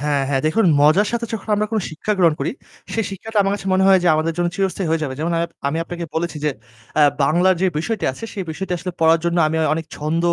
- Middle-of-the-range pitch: Yes, medium, 170 Hz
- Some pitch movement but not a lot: Yes, average, 3.6 semitones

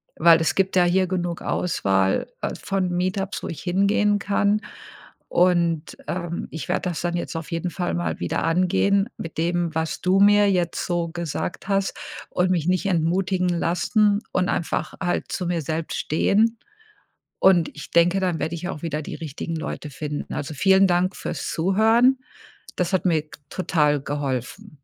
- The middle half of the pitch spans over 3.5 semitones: No, average, 2.9 semitones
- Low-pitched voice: No, medium, 175 Hz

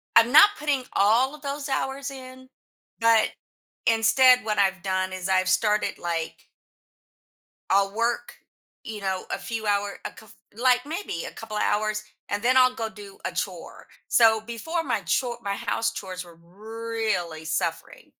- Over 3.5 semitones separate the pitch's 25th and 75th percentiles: Yes, average, 4.3 semitones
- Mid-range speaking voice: No, high, 220 Hz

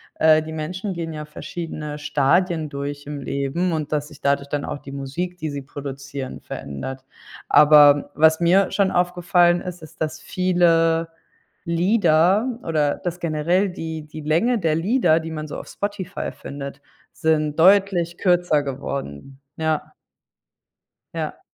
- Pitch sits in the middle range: Yes, medium, 160 Hz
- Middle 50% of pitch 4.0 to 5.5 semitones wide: No, average, 3.3 semitones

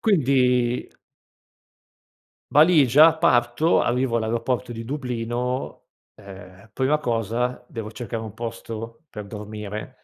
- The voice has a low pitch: Yes, low, 120 Hz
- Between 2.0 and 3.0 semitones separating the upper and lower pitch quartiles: Yes, average, 2.7 semitones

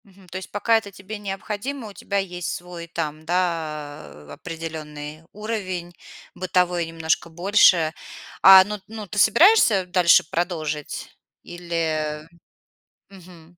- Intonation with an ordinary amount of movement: Yes, average, 3.5 semitones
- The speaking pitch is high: No, medium, 180 Hz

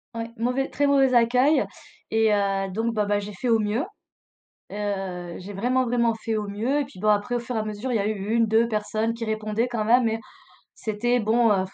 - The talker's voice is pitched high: Yes, high, 220 Hz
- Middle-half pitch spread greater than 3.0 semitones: No, narrow, 2.6 semitones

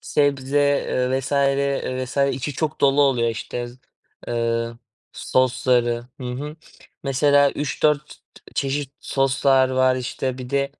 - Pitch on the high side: No, low, 130 Hz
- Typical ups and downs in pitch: No, narrow, 2.0 semitones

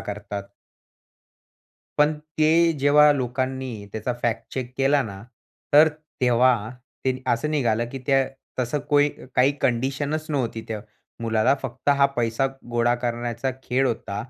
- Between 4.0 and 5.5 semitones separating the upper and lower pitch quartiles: No, average, 3.2 semitones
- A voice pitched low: Yes, low, 130 Hz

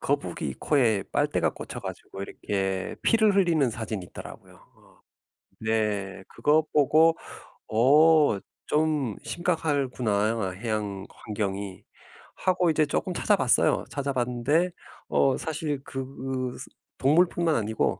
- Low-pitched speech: Yes, low, 130 Hz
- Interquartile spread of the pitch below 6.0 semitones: No, wide, 6.6 semitones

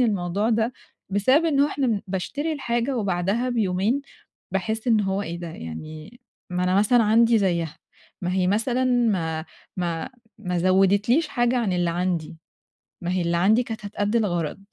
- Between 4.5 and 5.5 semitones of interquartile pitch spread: Yes, average, 4.8 semitones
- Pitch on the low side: No, high, 200 Hz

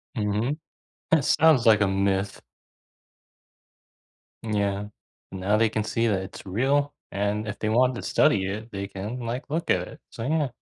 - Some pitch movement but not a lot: Yes, average, 4.2 semitones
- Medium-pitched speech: No, low, 110 Hz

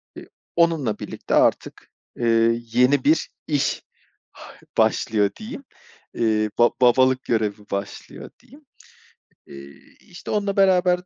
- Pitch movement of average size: No, wide, 8.1 semitones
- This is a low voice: Yes, low, 125 Hz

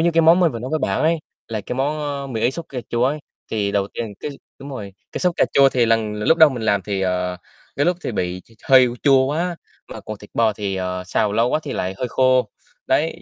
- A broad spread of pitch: Yes, wide, 5.8 semitones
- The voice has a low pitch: Yes, low, 120 Hz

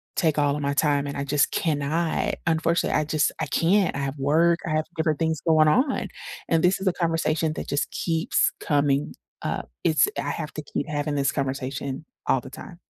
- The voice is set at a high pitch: No, medium, 155 Hz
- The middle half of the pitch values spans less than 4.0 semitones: Yes, narrow, 2.5 semitones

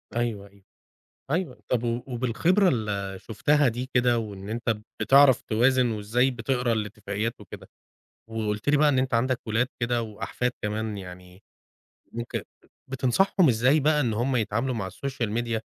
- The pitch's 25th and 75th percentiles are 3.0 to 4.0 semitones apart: Yes, average, 3.3 semitones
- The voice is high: No, low, 120 Hz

